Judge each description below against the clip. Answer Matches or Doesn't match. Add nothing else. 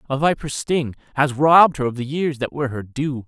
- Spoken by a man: Matches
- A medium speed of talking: Doesn't match